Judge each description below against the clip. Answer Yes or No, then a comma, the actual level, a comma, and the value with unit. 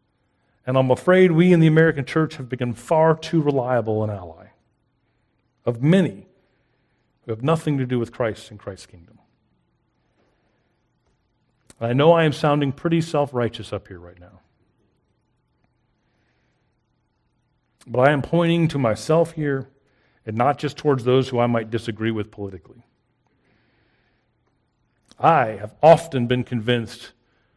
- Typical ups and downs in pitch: Yes, average, 3.9 semitones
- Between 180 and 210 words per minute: No, slow, 135 wpm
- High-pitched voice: No, low, 125 Hz